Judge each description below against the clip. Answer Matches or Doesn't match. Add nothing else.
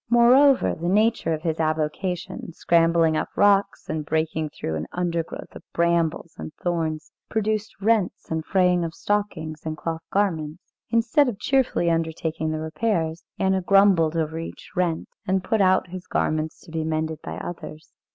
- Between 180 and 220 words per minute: Doesn't match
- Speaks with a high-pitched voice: Doesn't match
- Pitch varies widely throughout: Doesn't match